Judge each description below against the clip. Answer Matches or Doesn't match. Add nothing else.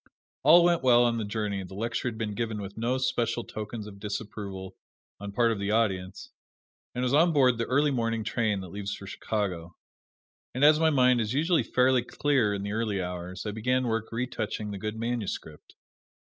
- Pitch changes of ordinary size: Matches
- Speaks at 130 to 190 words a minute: Doesn't match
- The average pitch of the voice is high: Doesn't match